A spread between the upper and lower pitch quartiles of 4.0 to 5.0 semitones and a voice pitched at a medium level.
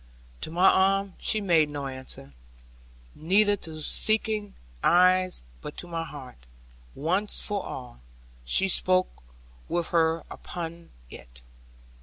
Yes: average, 4.6 semitones; medium, 170 Hz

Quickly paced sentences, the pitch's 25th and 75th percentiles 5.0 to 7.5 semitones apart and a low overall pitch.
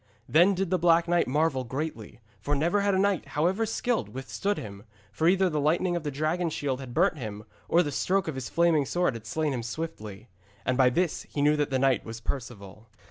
No: fast, 220 wpm; wide, 5.4 semitones; medium, 150 Hz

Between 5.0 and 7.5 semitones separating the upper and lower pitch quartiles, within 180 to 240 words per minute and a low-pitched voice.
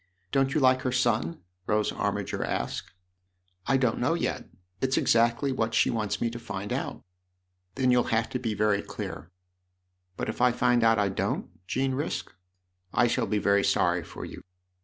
Yes: wide, 5.4 semitones; average, 200 wpm; low, 115 Hz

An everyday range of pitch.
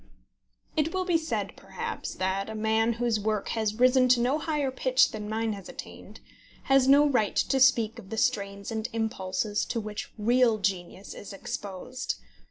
Yes: average, 3.6 semitones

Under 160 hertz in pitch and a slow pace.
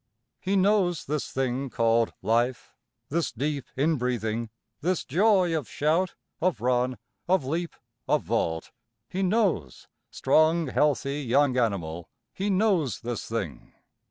Yes: medium, 140 Hz; slow, 125 wpm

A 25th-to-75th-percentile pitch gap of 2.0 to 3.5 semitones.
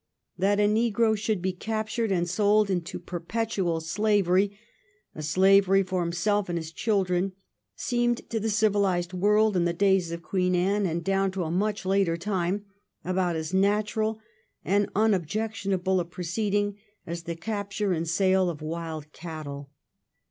Yes: average, 3.2 semitones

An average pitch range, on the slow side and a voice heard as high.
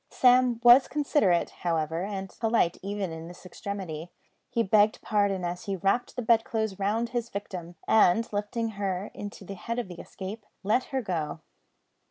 No: average, 4.0 semitones; average, 165 wpm; high, 200 Hz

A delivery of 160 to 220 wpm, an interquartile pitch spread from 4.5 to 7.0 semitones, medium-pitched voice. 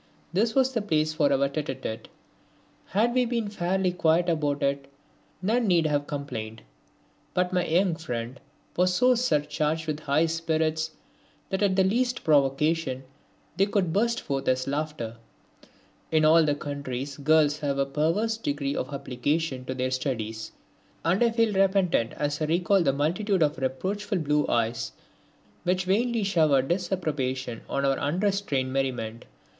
No: average, 150 wpm; wide, 5.4 semitones; medium, 155 Hz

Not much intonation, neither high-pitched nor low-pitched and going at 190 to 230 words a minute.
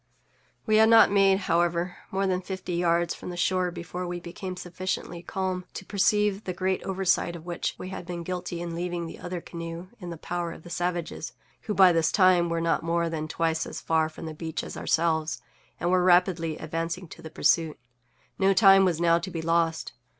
Yes: narrow, 1.8 semitones; medium, 175 Hz; fast, 205 wpm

